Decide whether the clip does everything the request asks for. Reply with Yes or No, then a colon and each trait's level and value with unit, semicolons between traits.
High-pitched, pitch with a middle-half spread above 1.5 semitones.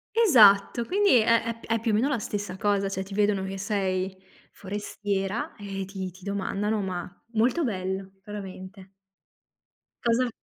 Yes: high, 200 Hz; average, 2.9 semitones